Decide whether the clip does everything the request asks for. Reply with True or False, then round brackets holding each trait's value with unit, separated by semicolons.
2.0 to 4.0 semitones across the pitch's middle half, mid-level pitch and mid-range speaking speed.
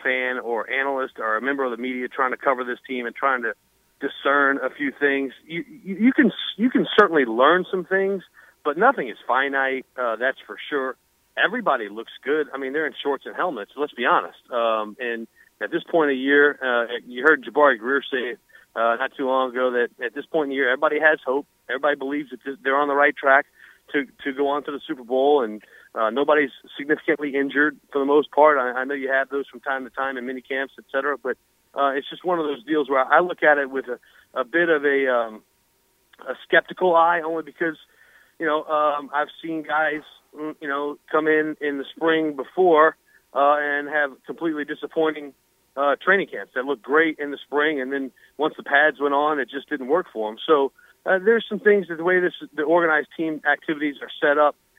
False (2.6 semitones; 145 Hz; 225 wpm)